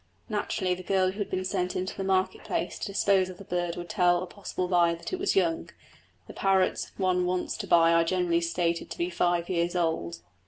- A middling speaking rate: No, fast, 225 wpm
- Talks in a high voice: No, medium, 180 Hz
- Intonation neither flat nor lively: No, narrow, 1.6 semitones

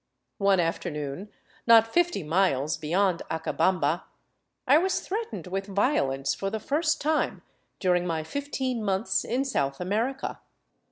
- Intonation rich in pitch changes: Yes, wide, 8.0 semitones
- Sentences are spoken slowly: Yes, slow, 125 wpm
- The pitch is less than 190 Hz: No, high, 195 Hz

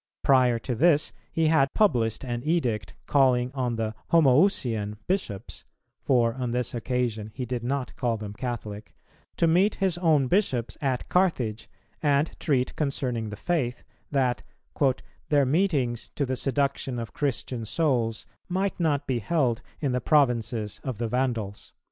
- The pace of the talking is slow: No, average, 150 wpm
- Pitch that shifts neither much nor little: Yes, average, 3.9 semitones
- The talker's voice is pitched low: Yes, low, 130 Hz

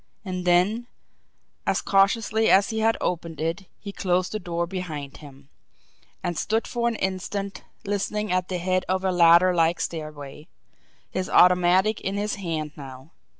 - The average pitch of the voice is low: No, medium, 185 Hz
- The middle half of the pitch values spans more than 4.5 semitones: No, average, 3.0 semitones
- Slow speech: No, average, 155 wpm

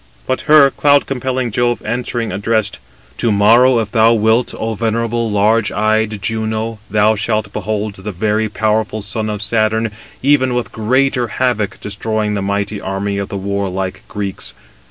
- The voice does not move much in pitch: Yes, narrow, 2.3 semitones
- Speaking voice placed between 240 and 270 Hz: No, low, 110 Hz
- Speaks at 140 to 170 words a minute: Yes, average, 155 wpm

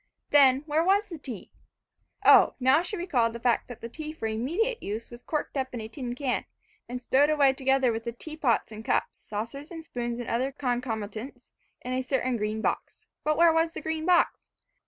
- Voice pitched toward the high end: Yes, very high, 260 Hz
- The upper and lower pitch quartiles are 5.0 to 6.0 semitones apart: No, average, 4.6 semitones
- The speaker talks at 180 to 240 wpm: Yes, average, 200 wpm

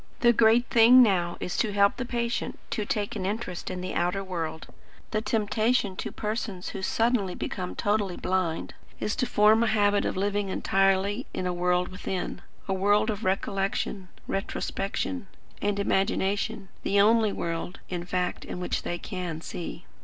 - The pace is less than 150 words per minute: No, average, 165 wpm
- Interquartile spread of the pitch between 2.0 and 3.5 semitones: Yes, average, 2.8 semitones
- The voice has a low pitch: No, high, 200 Hz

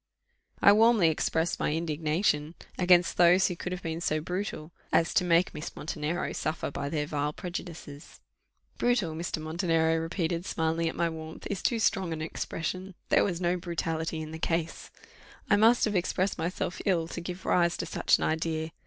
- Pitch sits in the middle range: Yes, medium, 170 Hz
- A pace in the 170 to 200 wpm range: Yes, average, 180 wpm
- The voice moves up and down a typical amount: No, narrow, 2.1 semitones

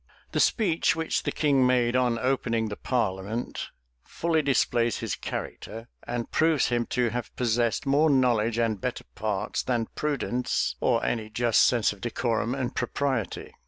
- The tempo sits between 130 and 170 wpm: Yes, average, 155 wpm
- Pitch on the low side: Yes, low, 120 Hz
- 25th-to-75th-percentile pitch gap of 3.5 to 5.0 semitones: No, narrow, 2.5 semitones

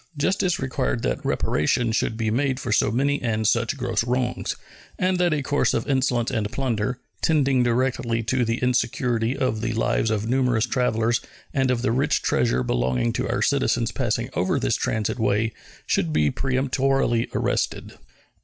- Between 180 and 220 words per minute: No, average, 165 wpm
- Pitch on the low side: Yes, low, 120 Hz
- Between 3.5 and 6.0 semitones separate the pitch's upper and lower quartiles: No, average, 2.9 semitones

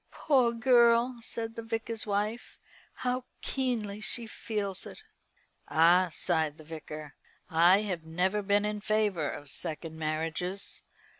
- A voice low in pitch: No, high, 205 Hz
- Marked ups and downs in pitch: Yes, wide, 5.8 semitones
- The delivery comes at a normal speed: No, slow, 130 wpm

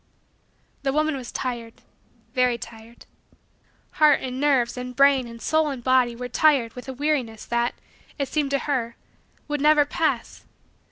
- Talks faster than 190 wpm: No, average, 155 wpm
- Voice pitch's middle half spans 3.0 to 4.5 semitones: Yes, average, 3.4 semitones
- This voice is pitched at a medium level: No, very high, 260 Hz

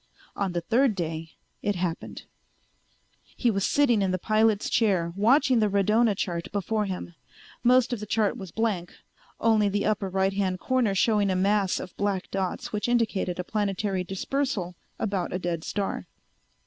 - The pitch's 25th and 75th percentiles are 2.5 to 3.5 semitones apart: Yes, average, 3.0 semitones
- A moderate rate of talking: Yes, average, 165 wpm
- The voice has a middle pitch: No, high, 200 Hz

